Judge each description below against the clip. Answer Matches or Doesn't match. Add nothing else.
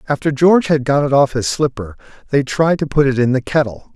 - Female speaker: Doesn't match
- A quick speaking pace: Matches